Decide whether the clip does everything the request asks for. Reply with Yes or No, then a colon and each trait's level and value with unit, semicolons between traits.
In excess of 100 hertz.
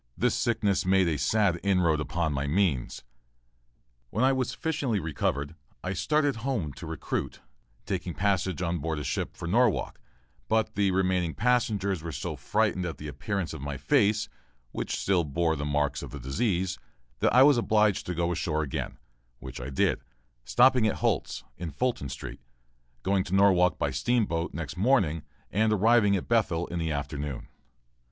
No: very low, 90 Hz